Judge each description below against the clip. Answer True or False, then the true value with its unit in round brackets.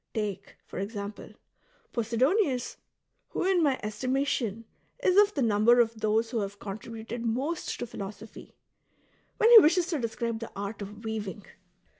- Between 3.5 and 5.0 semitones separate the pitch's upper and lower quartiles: True (4.0 semitones)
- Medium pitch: False (230 Hz)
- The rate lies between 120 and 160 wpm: True (155 wpm)